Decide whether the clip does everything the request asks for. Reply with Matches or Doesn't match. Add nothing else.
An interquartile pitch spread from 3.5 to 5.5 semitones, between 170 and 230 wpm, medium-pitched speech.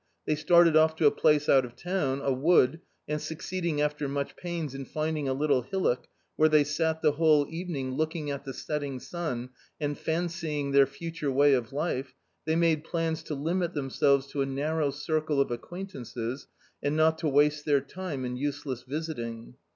Doesn't match